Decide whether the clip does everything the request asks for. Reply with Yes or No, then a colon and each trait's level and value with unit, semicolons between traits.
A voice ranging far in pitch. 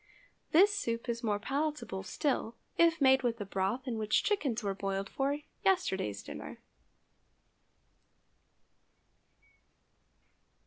Yes: wide, 6.5 semitones